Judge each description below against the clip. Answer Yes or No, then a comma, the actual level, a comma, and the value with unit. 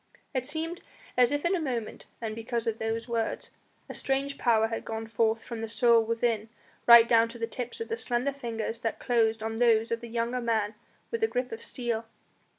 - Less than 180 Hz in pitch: No, high, 230 Hz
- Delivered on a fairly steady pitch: Yes, narrow, 1.9 semitones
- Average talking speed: No, fast, 210 wpm